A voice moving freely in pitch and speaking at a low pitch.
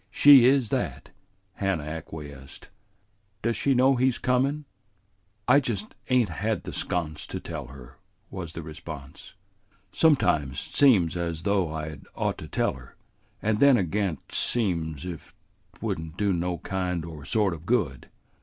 Yes: wide, 6.8 semitones; very low, 90 Hz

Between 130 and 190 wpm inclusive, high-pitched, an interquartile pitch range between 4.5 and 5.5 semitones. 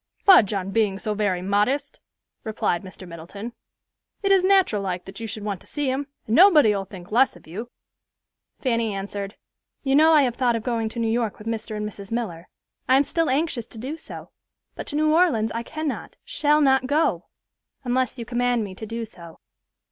No: average, 200 wpm; high, 230 Hz; average, 5.1 semitones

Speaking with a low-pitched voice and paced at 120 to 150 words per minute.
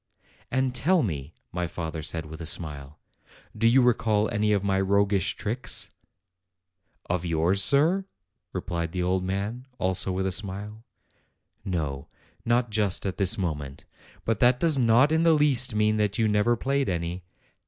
No: low, 100 Hz; average, 165 wpm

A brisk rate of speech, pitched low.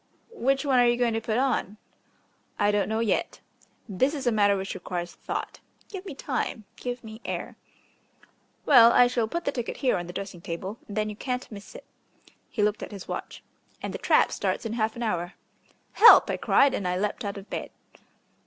No: fast, 210 wpm; high, 220 Hz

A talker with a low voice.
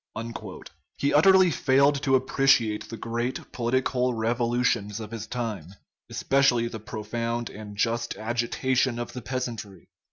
Yes: low, 120 Hz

